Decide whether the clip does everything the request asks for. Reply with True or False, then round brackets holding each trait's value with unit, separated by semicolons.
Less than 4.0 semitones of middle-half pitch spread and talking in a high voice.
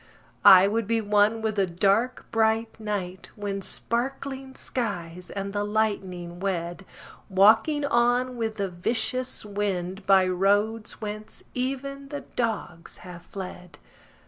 True (3.4 semitones; 210 Hz)